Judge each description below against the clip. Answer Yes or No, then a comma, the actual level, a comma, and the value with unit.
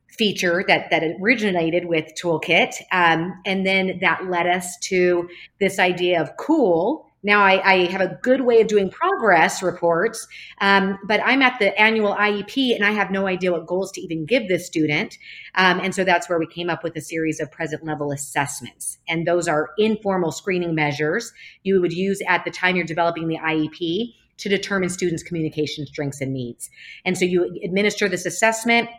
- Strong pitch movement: No, average, 3.2 semitones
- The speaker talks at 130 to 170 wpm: No, average, 190 wpm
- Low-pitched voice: No, medium, 180 Hz